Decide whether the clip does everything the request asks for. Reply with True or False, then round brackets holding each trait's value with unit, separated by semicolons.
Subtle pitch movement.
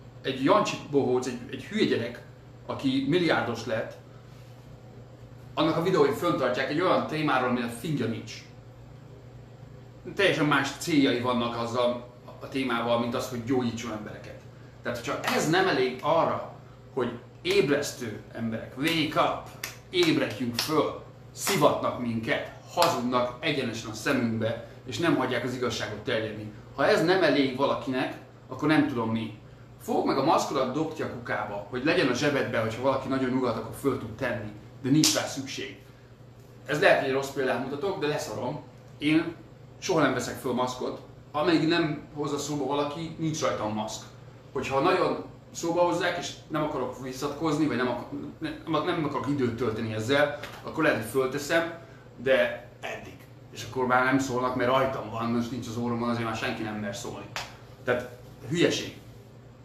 True (2.2 semitones)